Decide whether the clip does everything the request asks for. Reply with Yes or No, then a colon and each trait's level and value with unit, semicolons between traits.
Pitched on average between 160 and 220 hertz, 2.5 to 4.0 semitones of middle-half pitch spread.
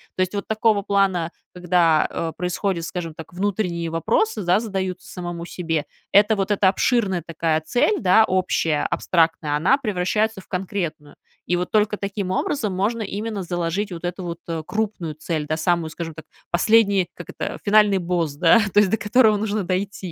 Yes: medium, 185 Hz; average, 3.5 semitones